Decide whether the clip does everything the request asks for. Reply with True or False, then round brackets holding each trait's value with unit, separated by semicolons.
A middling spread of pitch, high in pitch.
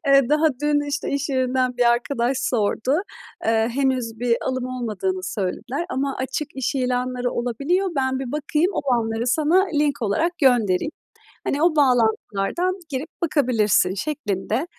True (3.8 semitones; 255 Hz)